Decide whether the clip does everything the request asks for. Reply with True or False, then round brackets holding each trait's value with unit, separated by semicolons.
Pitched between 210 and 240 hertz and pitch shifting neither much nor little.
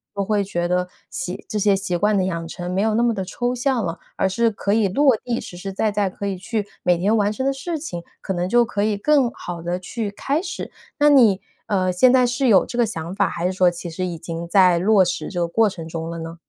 False (200 Hz; 4.4 semitones)